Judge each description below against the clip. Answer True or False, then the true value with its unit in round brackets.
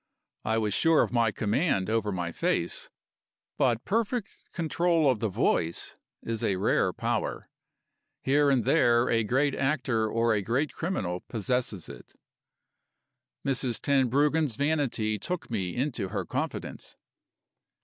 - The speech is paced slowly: True (130 wpm)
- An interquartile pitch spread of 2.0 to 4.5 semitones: False (5.1 semitones)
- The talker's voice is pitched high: False (120 Hz)